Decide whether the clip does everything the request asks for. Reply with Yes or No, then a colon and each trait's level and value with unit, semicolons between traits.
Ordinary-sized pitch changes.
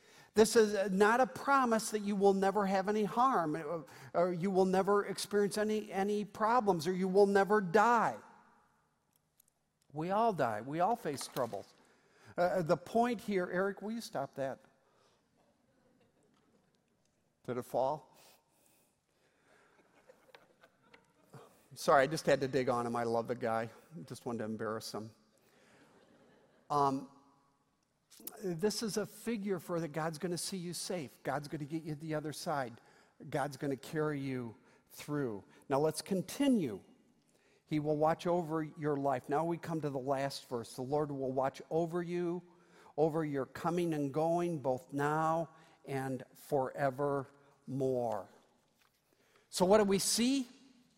No: wide, 6.1 semitones